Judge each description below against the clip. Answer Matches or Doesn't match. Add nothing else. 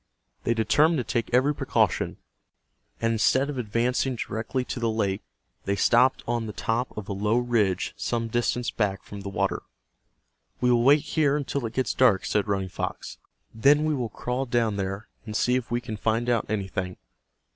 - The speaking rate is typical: Matches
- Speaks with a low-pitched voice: Matches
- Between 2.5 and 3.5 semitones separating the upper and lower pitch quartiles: Matches